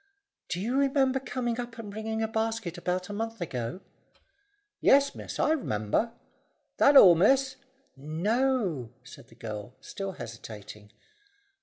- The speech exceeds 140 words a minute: No, slow, 135 wpm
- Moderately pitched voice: No, high, 210 Hz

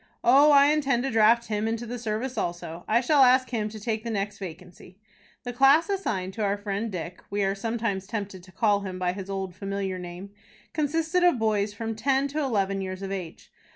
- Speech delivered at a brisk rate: Yes, fast, 215 wpm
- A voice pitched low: No, high, 215 Hz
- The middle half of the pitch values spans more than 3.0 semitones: Yes, average, 4.1 semitones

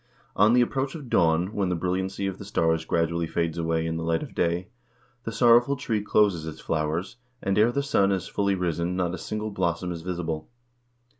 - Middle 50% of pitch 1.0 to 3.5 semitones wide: No, average, 4.1 semitones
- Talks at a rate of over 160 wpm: Yes, fast, 205 wpm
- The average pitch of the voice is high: No, very low, 90 Hz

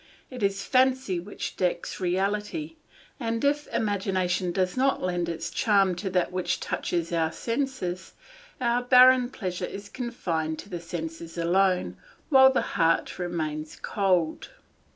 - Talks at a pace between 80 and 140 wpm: Yes, slow, 135 wpm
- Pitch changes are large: Yes, wide, 5.7 semitones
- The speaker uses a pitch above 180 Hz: Yes, high, 190 Hz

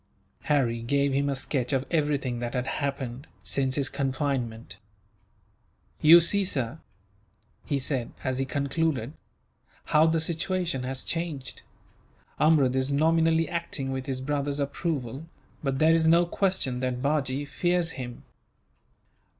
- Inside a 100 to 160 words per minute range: Yes, slow, 135 wpm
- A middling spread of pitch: Yes, average, 3.6 semitones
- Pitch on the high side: No, medium, 140 Hz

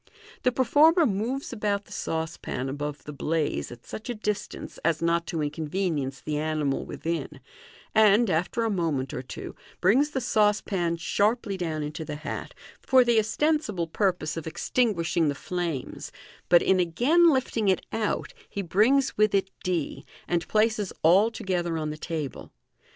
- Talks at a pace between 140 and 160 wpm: Yes, average, 155 wpm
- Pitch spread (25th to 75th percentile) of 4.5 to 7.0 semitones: Yes, wide, 5.5 semitones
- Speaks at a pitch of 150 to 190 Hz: Yes, medium, 185 Hz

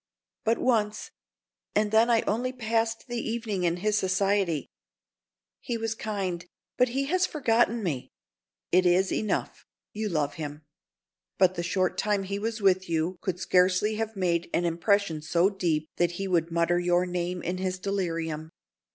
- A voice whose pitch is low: No, high, 190 Hz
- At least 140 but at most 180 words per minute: Yes, average, 160 wpm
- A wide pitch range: No, average, 4.0 semitones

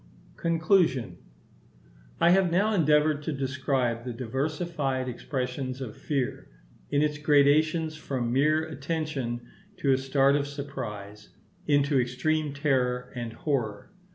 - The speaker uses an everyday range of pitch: Yes, average, 3.6 semitones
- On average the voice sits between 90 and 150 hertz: Yes, medium, 140 Hz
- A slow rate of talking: Yes, slow, 115 wpm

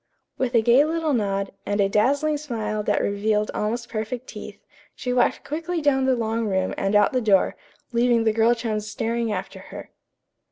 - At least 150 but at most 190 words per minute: Yes, average, 185 wpm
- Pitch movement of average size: Yes, average, 3.3 semitones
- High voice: Yes, high, 230 Hz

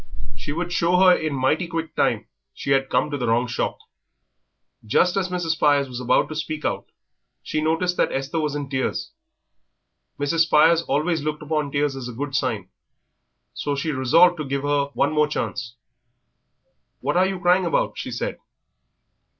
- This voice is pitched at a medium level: Yes, medium, 150 Hz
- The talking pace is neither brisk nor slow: Yes, average, 175 wpm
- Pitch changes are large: No, average, 3.5 semitones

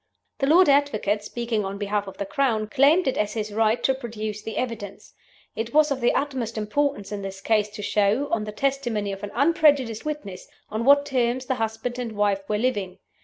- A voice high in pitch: Yes, high, 225 Hz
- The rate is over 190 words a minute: Yes, fast, 205 wpm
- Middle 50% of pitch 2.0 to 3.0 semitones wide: No, average, 4.4 semitones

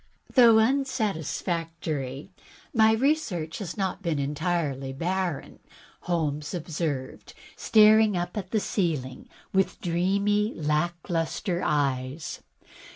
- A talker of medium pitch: Yes, medium, 175 Hz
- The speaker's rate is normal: No, slow, 95 wpm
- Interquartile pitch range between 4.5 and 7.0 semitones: Yes, average, 5.3 semitones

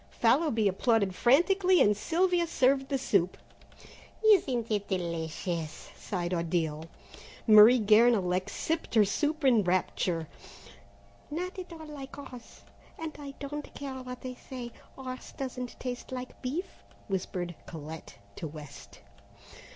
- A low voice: No, high, 245 Hz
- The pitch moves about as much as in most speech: No, wide, 7.4 semitones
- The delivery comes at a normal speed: No, slow, 125 wpm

